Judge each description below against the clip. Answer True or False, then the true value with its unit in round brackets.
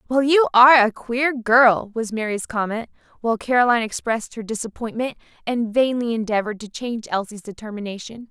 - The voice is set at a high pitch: True (230 Hz)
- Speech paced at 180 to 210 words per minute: False (150 wpm)